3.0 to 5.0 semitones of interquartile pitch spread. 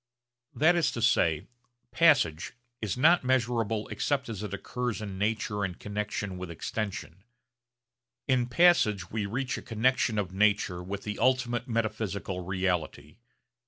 Yes: average, 4.3 semitones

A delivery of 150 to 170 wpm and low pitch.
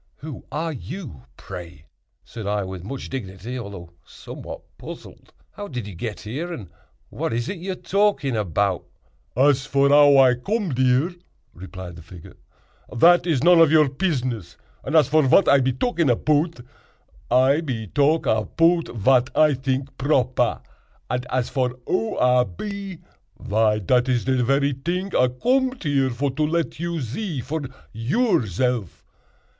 Yes: average, 160 wpm; low, 130 Hz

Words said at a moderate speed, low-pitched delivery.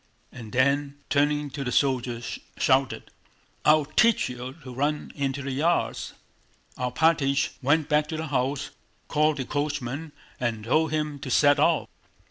No: average, 145 wpm; medium, 145 Hz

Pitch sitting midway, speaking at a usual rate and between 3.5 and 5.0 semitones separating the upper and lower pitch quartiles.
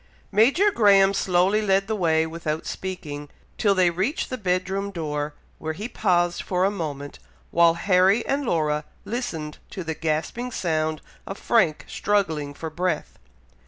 Yes: medium, 180 Hz; average, 155 wpm; average, 4.1 semitones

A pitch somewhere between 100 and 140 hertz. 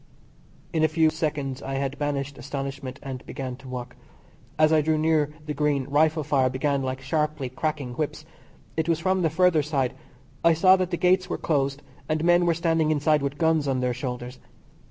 No: medium, 150 Hz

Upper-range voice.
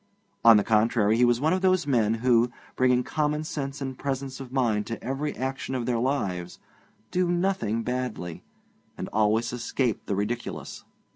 No: low, 125 Hz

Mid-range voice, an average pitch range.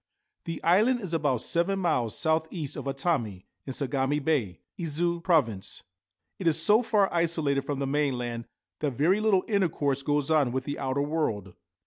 Yes: medium, 150 Hz; average, 4.2 semitones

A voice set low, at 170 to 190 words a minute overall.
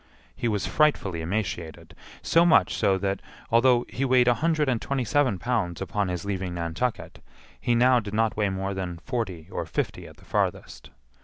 Yes: low, 105 Hz; average, 180 wpm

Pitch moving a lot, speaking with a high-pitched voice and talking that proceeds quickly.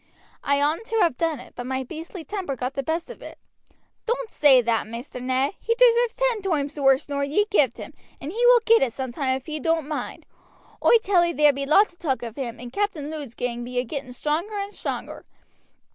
Yes: wide, 6.5 semitones; very high, 295 Hz; fast, 225 wpm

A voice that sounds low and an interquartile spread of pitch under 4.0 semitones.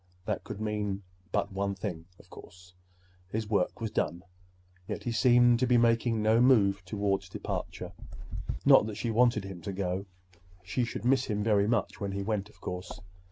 Yes: low, 105 Hz; average, 3.0 semitones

